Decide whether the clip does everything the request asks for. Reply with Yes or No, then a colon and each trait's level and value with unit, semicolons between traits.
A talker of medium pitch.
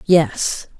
Yes: medium, 155 Hz